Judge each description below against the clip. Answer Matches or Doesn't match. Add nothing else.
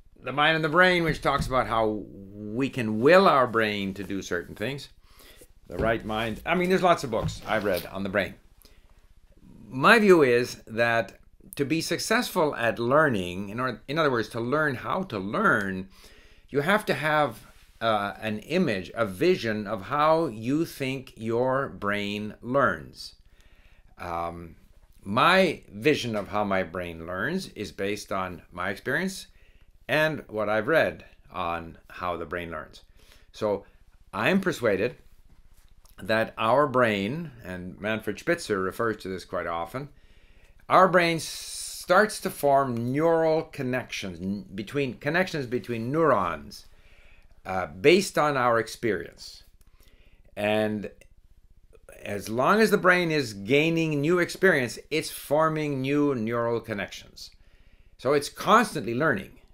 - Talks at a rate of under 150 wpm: Matches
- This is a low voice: Matches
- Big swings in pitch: Matches